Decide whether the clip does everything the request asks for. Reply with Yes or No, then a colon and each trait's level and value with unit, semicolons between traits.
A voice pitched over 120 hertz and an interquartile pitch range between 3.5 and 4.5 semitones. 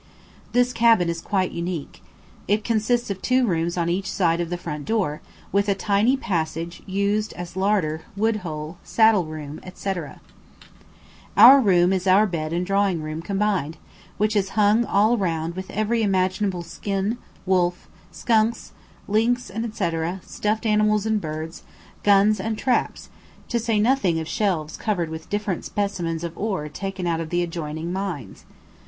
Yes: high, 190 Hz; average, 4.0 semitones